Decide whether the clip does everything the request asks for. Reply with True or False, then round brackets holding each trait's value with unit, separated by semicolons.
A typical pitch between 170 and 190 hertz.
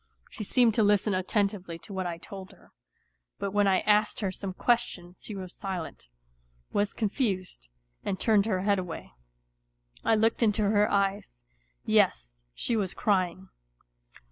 False (200 Hz)